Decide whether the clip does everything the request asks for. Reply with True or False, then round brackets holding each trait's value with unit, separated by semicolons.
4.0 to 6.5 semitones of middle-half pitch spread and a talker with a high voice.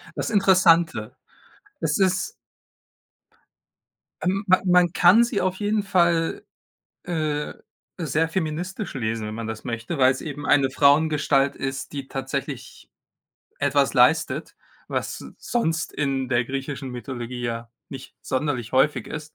False (5.1 semitones; 145 Hz)